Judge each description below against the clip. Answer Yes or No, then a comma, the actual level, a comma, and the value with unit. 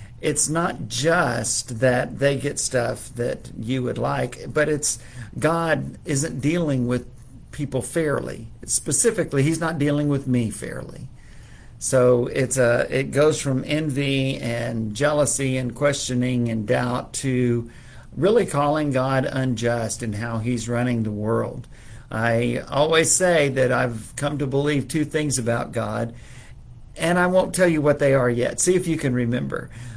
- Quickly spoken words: No, average, 150 wpm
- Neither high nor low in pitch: No, low, 130 Hz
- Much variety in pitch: No, average, 3.6 semitones